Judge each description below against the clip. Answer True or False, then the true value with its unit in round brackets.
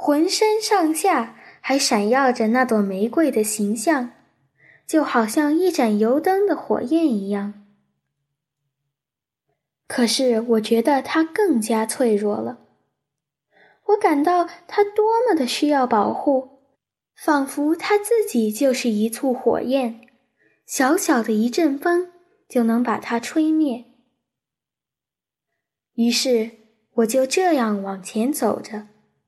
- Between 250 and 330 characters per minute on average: False (170 characters per minute)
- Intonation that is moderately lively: False (6.1 semitones)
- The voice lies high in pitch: True (255 Hz)